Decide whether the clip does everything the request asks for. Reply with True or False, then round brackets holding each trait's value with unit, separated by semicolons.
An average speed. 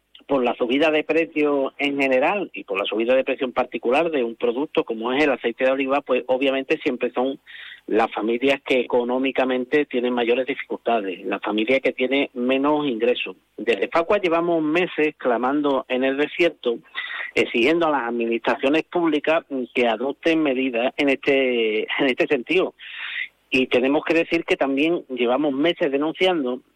True (160 wpm)